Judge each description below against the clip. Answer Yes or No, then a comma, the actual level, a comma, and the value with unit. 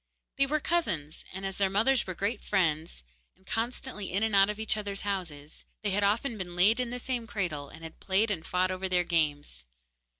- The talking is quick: Yes, fast, 210 wpm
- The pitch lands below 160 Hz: No, high, 195 Hz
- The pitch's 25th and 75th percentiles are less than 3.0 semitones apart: No, average, 4.0 semitones